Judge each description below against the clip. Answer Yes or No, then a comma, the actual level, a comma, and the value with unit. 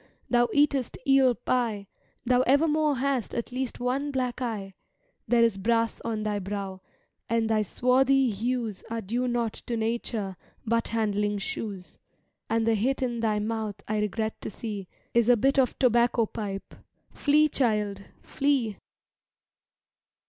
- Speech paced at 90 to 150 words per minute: Yes, average, 140 wpm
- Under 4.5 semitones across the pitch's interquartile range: Yes, average, 3.1 semitones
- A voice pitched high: Yes, high, 230 Hz